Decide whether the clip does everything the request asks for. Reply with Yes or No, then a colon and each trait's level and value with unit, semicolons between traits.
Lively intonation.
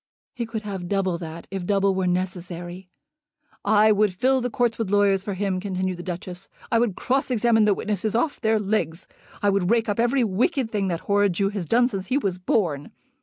No: average, 3.3 semitones